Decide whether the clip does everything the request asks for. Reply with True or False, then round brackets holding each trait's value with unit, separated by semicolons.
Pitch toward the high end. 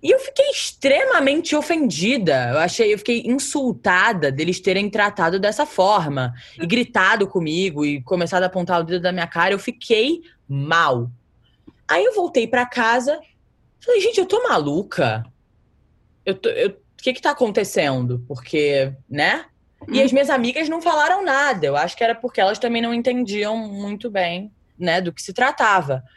True (210 Hz)